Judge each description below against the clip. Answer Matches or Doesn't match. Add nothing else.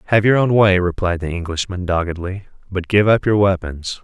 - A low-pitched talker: Matches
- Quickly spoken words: Doesn't match